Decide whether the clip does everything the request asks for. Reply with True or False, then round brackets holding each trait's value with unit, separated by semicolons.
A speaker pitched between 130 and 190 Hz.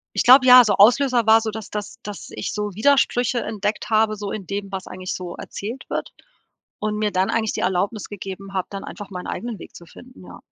False (210 Hz)